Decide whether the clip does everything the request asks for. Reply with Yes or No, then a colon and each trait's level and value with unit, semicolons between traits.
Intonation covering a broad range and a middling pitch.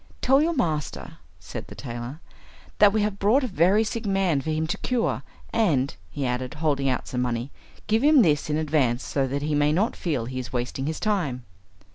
Yes: wide, 7.9 semitones; medium, 155 Hz